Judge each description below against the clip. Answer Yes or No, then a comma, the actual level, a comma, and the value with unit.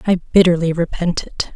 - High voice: No, medium, 170 Hz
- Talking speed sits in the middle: Yes, average, 155 wpm